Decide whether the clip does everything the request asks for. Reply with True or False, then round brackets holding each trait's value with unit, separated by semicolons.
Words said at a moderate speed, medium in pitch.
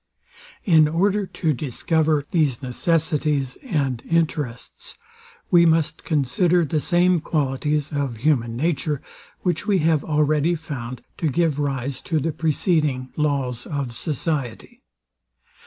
False (120 wpm; 150 Hz)